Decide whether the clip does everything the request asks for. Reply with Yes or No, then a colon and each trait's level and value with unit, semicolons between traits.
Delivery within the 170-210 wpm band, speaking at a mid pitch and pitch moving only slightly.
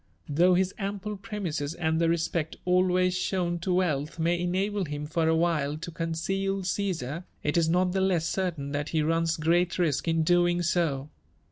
Yes: average, 175 wpm; medium, 170 Hz; narrow, 2.3 semitones